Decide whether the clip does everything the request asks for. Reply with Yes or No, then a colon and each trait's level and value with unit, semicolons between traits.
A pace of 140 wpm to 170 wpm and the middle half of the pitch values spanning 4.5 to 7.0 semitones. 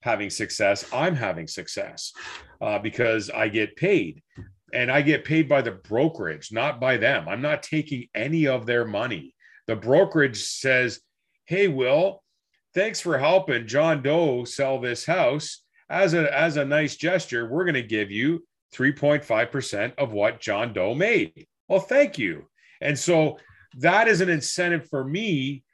Yes: average, 160 wpm; average, 4.9 semitones